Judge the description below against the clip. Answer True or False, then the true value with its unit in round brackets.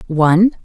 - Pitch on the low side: False (180 Hz)